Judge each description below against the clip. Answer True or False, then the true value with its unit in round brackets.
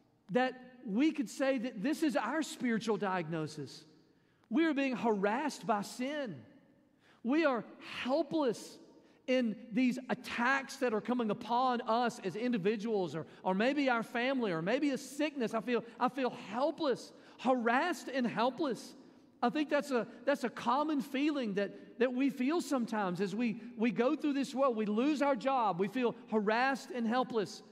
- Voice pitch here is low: False (245 Hz)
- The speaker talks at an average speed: True (160 wpm)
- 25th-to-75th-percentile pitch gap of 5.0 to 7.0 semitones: False (3.7 semitones)